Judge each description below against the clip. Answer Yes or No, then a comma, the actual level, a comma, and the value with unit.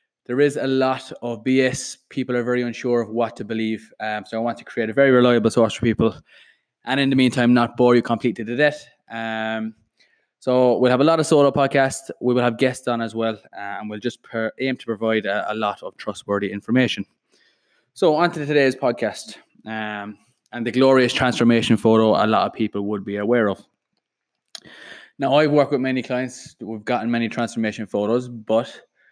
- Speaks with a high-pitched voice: No, low, 120 Hz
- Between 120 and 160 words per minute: No, average, 200 wpm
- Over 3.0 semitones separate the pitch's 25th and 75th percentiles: No, narrow, 2.6 semitones